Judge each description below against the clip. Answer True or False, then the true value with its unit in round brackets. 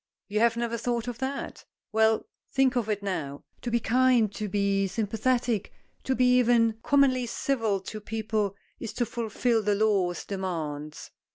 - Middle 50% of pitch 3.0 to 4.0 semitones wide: True (3.3 semitones)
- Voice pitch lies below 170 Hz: False (225 Hz)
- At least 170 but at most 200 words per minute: False (160 wpm)